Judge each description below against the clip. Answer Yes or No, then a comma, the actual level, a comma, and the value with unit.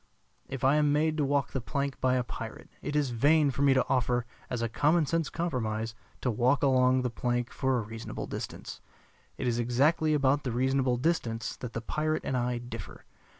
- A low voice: Yes, low, 130 Hz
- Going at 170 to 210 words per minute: Yes, average, 200 wpm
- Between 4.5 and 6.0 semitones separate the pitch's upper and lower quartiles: No, average, 3.1 semitones